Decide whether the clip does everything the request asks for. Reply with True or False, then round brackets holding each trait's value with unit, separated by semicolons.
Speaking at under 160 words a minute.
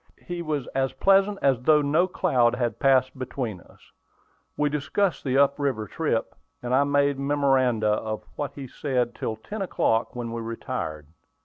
False (170 wpm)